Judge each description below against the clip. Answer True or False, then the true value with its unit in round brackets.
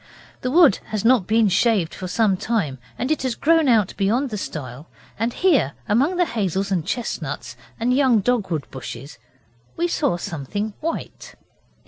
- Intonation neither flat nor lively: False (6.5 semitones)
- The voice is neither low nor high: False (215 Hz)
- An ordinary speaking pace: True (160 wpm)